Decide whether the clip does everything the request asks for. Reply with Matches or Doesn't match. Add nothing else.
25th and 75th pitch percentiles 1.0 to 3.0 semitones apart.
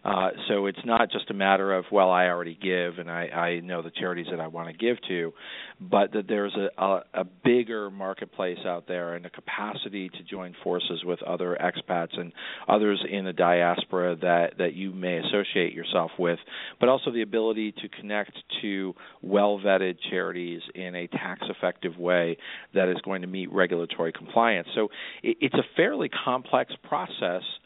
Matches